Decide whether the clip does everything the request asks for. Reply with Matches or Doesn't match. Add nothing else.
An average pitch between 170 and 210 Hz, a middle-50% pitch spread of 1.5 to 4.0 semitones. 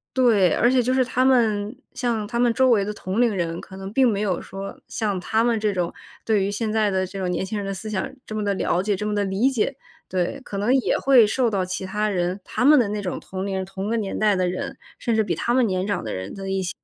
Matches